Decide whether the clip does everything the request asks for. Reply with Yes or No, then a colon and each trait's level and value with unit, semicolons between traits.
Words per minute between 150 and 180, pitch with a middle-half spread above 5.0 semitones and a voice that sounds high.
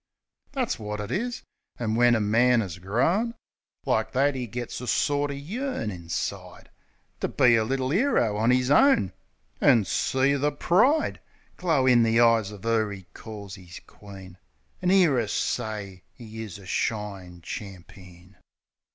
No: average, 155 wpm; wide, 5.5 semitones; low, 115 Hz